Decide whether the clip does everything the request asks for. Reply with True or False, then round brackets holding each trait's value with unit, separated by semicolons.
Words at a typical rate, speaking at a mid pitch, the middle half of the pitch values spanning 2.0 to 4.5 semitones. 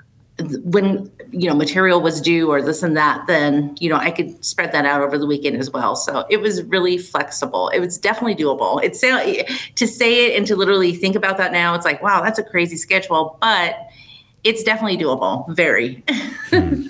False (195 wpm; 175 Hz; 5.6 semitones)